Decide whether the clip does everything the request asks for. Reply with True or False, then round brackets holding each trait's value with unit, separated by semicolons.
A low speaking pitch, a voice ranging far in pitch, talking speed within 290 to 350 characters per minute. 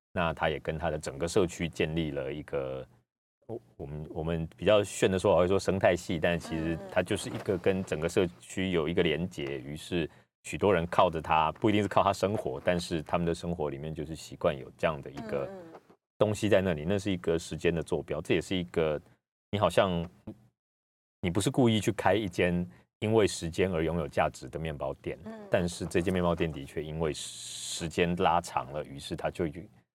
False (85 Hz; 3.1 semitones; 300 characters per minute)